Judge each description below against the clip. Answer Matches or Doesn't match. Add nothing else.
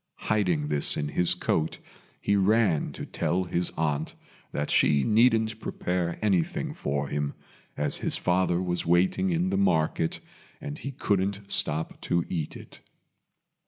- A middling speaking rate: Matches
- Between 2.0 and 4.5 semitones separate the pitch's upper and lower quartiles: Doesn't match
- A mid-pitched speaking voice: Doesn't match